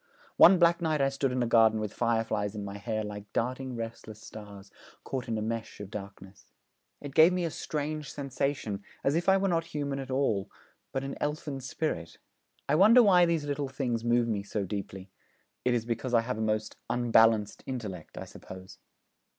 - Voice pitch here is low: Yes, low, 120 Hz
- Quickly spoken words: No, average, 190 wpm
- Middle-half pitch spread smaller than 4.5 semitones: No, average, 5.1 semitones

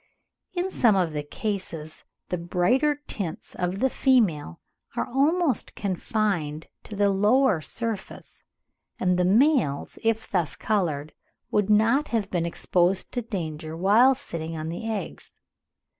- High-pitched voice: Yes, high, 195 Hz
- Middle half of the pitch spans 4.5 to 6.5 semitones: Yes, wide, 5.5 semitones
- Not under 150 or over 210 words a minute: No, slow, 135 wpm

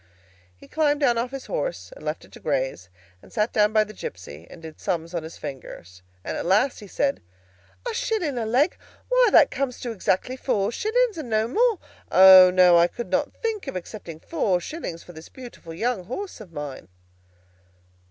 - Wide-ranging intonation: Yes, wide, 8.8 semitones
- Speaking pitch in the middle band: No, high, 215 Hz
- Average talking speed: Yes, average, 195 wpm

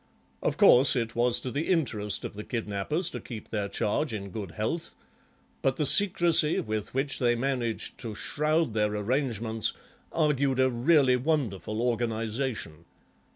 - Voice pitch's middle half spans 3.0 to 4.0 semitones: No, average, 4.7 semitones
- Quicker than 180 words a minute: No, average, 150 wpm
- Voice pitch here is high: No, low, 120 Hz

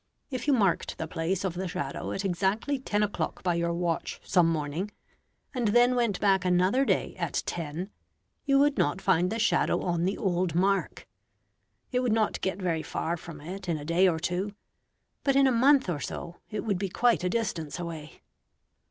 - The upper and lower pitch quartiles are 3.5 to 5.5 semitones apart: Yes, average, 4.4 semitones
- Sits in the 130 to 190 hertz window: Yes, medium, 185 Hz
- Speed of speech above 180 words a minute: Yes, average, 195 wpm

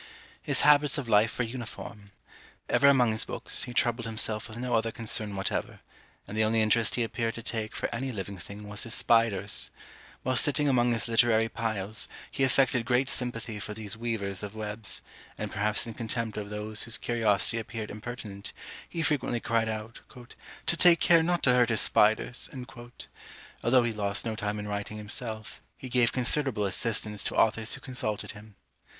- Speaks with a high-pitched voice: No, low, 115 Hz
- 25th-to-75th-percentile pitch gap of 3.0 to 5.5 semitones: No, narrow, 2.5 semitones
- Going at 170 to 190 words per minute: Yes, average, 180 wpm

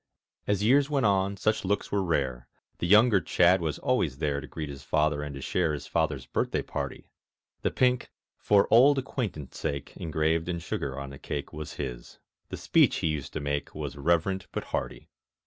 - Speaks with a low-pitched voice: Yes, very low, 80 Hz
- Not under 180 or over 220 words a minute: Yes, average, 190 wpm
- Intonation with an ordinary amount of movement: No, wide, 5.9 semitones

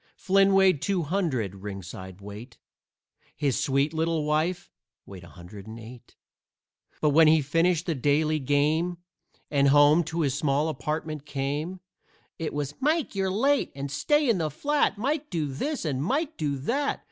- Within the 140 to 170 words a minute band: Yes, average, 160 wpm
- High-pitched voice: No, medium, 155 Hz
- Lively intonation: No, average, 4.9 semitones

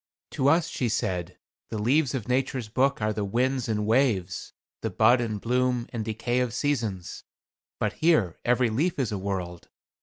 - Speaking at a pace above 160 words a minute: Yes, average, 175 wpm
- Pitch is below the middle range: Yes, low, 120 Hz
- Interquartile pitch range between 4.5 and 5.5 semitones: No, average, 3.8 semitones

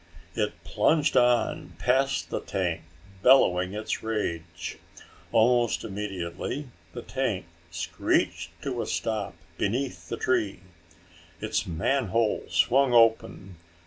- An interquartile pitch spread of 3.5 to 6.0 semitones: Yes, wide, 5.4 semitones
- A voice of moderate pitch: No, low, 110 Hz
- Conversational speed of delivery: No, slow, 105 wpm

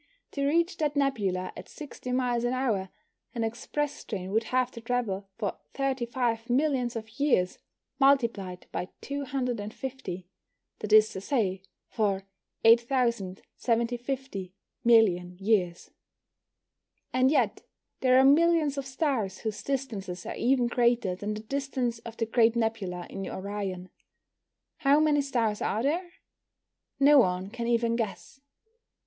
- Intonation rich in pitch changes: No, average, 4.8 semitones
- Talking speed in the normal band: No, slow, 130 wpm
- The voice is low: No, high, 235 Hz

